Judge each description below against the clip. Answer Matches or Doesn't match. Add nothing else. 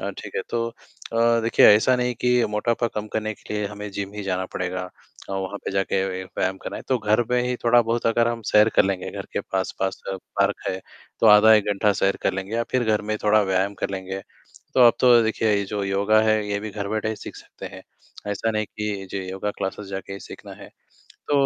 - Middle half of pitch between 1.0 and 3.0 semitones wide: Matches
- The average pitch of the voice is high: Doesn't match